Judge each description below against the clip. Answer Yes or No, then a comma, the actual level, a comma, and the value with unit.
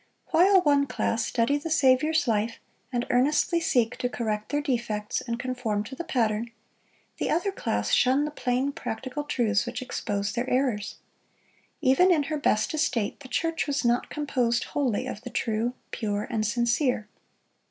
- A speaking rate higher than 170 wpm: No, average, 165 wpm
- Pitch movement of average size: Yes, average, 4.3 semitones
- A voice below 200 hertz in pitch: No, very high, 250 Hz